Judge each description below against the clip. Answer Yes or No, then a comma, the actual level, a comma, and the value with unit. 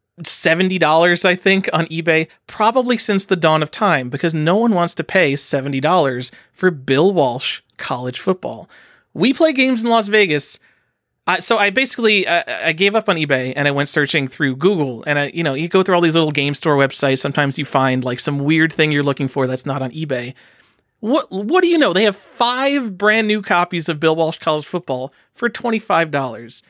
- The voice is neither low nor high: Yes, medium, 165 Hz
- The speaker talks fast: Yes, fast, 210 wpm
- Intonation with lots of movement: Yes, wide, 5.9 semitones